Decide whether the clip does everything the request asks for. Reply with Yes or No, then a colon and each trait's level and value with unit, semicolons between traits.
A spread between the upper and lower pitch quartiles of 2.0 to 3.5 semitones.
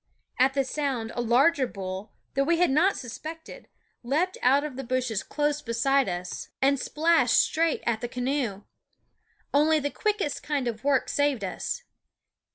No: average, 3.9 semitones